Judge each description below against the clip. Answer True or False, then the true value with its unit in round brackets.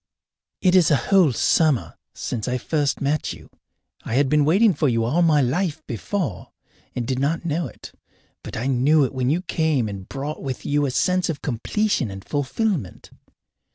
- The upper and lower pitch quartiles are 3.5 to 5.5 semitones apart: True (4.5 semitones)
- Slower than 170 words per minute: False (185 wpm)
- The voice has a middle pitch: True (145 Hz)